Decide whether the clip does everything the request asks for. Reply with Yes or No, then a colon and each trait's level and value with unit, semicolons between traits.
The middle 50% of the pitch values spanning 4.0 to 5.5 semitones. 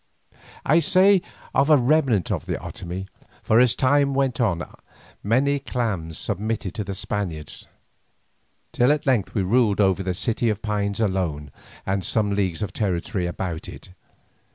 Yes: average, 5.2 semitones